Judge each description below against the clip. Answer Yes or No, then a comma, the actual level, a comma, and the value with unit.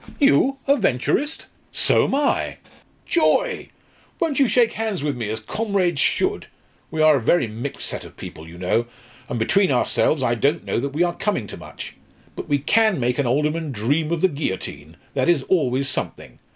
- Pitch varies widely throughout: Yes, wide, 8.4 semitones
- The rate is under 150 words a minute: No, average, 190 wpm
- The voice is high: No, medium, 150 Hz